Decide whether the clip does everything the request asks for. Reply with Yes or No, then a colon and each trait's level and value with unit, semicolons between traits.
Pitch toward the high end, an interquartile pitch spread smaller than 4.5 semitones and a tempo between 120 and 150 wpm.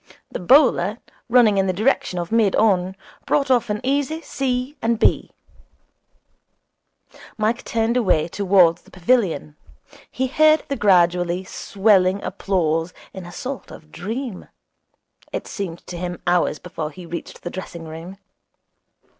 No: high, 195 Hz; average, 5.1 semitones; average, 140 wpm